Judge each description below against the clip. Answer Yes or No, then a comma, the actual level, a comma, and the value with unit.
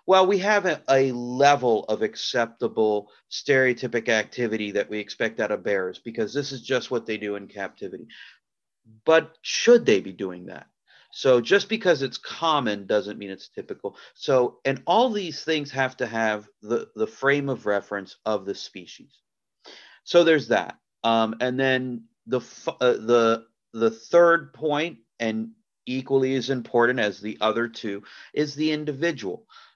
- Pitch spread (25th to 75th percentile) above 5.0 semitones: Yes, wide, 5.6 semitones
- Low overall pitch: Yes, low, 125 Hz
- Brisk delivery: No, average, 160 wpm